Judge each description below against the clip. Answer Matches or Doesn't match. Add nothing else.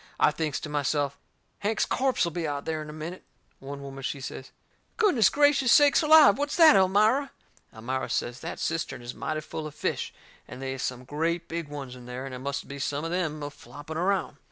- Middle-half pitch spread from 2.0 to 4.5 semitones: Doesn't match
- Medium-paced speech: Doesn't match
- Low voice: Doesn't match